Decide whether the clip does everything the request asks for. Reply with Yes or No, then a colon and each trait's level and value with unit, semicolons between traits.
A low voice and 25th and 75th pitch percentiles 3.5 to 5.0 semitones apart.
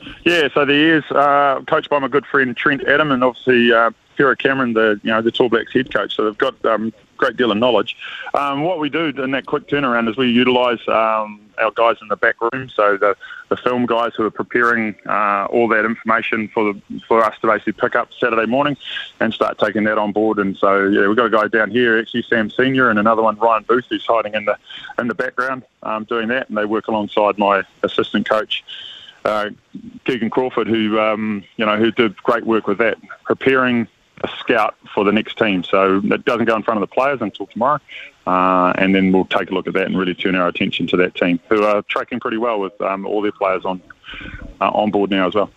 No: low, 110 Hz; average, 2.9 semitones